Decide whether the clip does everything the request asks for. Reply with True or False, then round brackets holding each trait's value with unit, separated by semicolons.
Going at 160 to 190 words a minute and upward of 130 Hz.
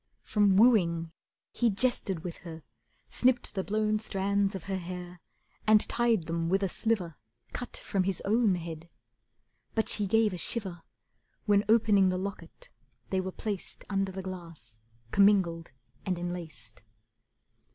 False (140 wpm; 190 Hz)